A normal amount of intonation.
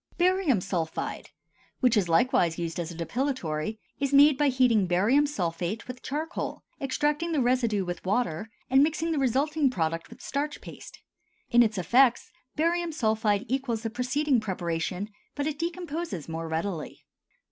No: wide, 8.1 semitones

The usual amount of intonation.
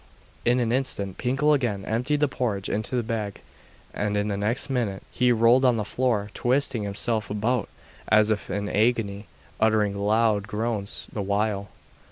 Yes: average, 3.1 semitones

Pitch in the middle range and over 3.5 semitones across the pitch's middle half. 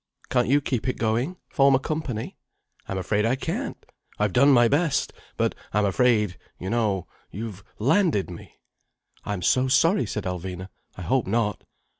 No: low, 115 Hz; average, 5.2 semitones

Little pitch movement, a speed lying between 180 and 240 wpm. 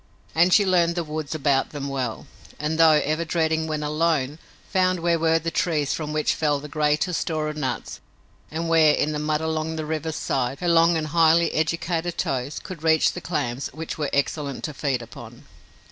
Yes: narrow, 1.8 semitones; average, 195 wpm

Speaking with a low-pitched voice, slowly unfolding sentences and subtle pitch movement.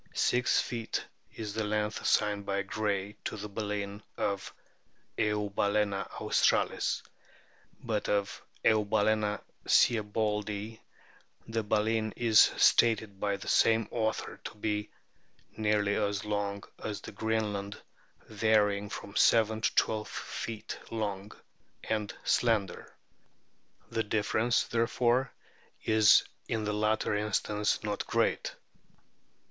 Yes: low, 105 Hz; slow, 115 wpm; narrow, 1.2 semitones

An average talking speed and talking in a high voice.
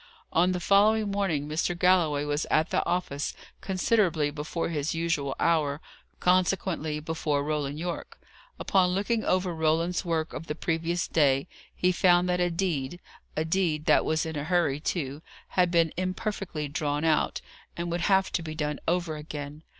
No: average, 165 wpm; medium, 165 Hz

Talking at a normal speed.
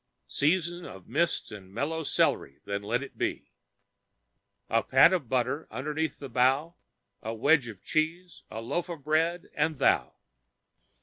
Yes: average, 145 wpm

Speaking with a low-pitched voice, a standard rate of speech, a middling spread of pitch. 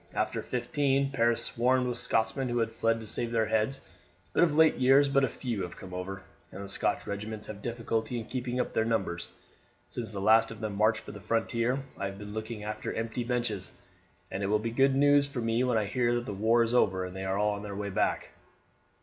No: low, 115 Hz; fast, 225 wpm; average, 3.0 semitones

